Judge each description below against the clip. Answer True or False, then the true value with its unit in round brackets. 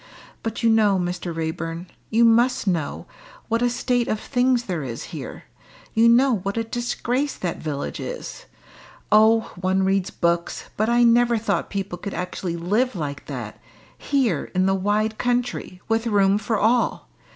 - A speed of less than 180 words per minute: True (165 wpm)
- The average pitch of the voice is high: True (215 Hz)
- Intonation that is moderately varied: True (4.6 semitones)